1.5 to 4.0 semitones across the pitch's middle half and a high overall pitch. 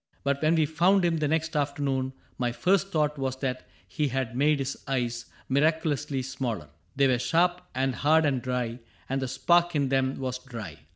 No: average, 3.4 semitones; low, 135 Hz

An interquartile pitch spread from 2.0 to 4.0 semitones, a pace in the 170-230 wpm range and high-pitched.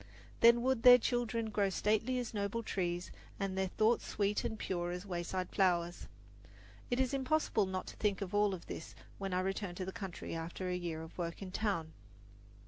Yes: average, 3.6 semitones; average, 190 wpm; high, 195 Hz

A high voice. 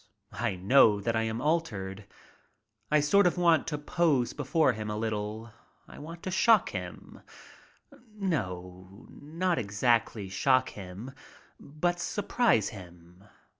No: low, 120 Hz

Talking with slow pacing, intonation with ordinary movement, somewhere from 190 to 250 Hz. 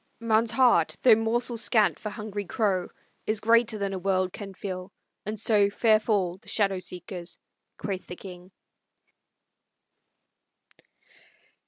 Yes: slow, 130 wpm; average, 3.0 semitones; high, 205 Hz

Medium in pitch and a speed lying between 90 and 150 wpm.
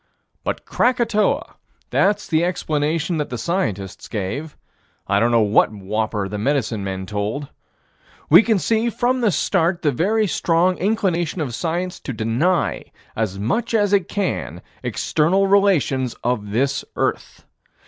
Yes: medium, 160 Hz; average, 140 wpm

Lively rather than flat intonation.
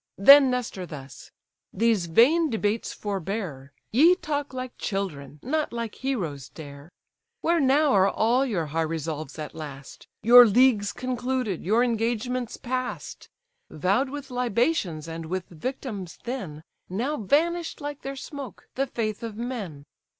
Yes: wide, 7.2 semitones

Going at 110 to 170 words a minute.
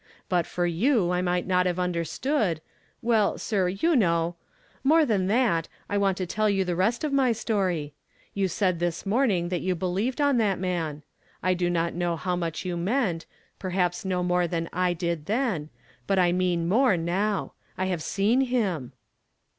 No: average, 185 wpm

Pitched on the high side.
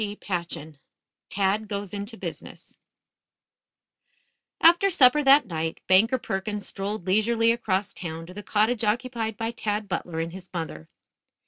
Yes: high, 205 Hz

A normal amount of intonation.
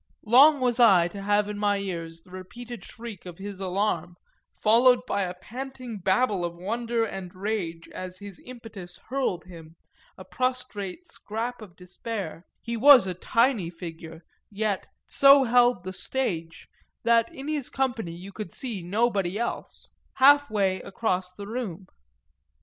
Yes: average, 4.8 semitones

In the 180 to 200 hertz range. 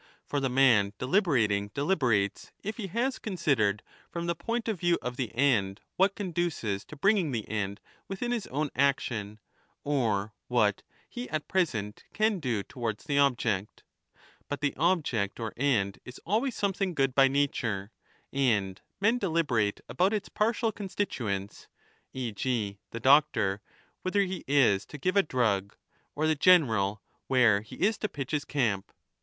No: low, 135 Hz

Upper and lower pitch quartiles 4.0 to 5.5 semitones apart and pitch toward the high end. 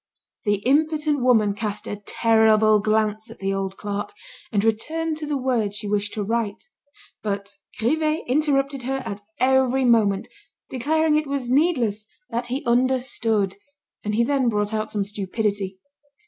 Yes: average, 4.4 semitones; high, 225 Hz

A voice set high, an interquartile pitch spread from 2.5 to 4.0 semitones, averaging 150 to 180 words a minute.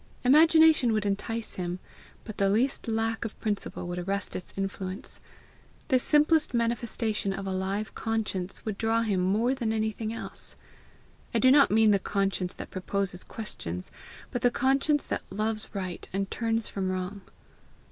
Yes: high, 215 Hz; average, 3.1 semitones; average, 155 wpm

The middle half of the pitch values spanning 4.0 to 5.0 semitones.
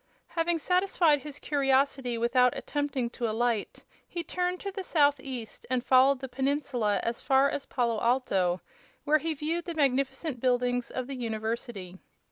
No: average, 3.6 semitones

